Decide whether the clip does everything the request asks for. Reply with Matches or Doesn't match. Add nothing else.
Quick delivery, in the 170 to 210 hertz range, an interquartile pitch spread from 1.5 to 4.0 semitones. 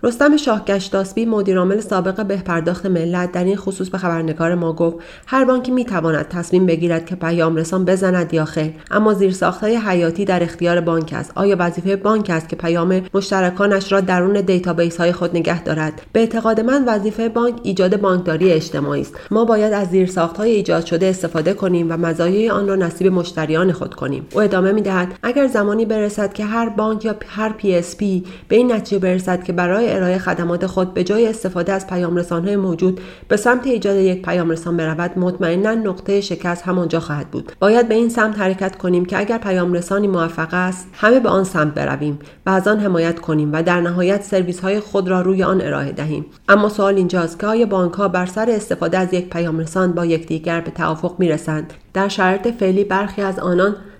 Matches